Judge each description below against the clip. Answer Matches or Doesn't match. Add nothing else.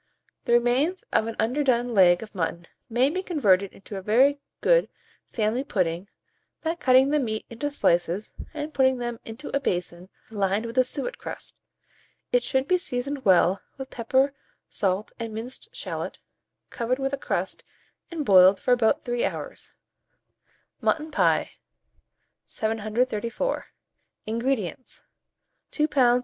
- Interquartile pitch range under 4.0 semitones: Doesn't match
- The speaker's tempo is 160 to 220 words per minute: Doesn't match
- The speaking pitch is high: Matches